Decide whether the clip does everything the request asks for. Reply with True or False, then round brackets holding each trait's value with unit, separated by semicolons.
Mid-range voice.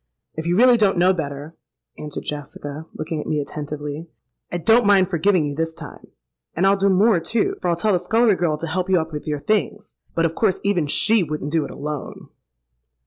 True (170 Hz)